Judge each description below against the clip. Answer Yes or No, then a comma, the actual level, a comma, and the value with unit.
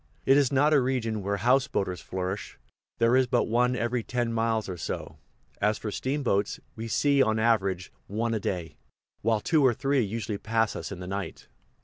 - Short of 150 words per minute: No, average, 195 wpm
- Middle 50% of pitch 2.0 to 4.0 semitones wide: Yes, average, 3.7 semitones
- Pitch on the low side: Yes, low, 115 Hz